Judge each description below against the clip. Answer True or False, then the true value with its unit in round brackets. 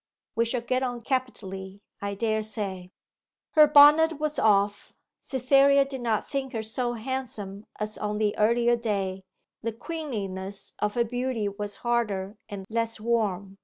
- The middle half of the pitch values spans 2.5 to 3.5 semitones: False (3.9 semitones)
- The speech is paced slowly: False (150 wpm)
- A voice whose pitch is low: False (225 Hz)